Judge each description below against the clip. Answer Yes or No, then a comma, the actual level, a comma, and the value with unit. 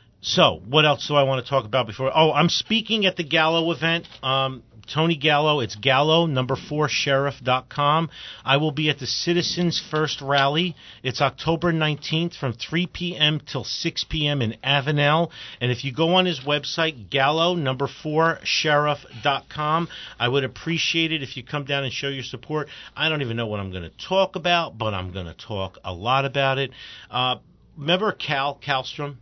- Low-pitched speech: No, medium, 145 Hz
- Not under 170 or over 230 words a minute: Yes, average, 190 wpm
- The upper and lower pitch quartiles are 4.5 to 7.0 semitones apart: No, average, 3.8 semitones